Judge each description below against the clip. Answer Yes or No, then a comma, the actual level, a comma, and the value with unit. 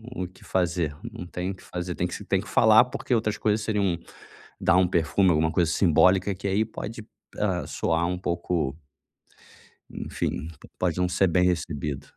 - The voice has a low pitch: Yes, very low, 90 Hz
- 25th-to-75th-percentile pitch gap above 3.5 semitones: No, average, 2.7 semitones